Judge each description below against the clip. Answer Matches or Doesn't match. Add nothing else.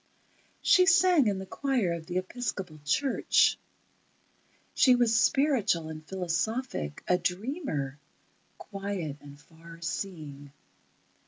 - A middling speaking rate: Doesn't match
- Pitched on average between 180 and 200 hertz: Matches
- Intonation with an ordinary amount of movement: Doesn't match